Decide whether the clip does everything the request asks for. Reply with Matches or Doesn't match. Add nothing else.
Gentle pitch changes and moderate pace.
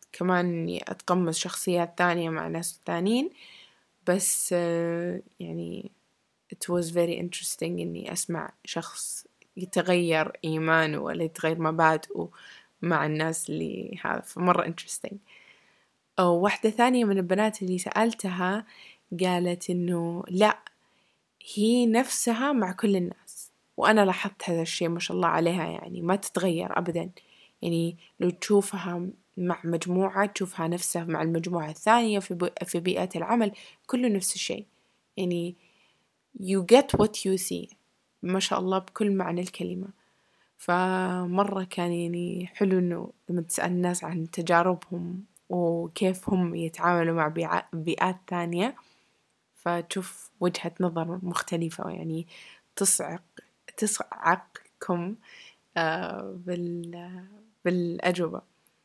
Matches